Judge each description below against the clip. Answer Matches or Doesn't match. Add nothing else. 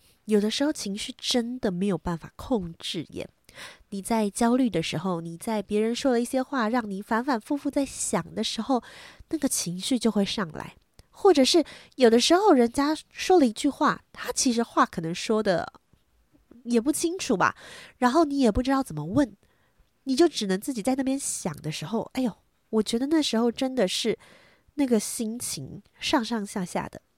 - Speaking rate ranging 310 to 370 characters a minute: Doesn't match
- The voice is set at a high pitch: Matches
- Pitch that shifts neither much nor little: Matches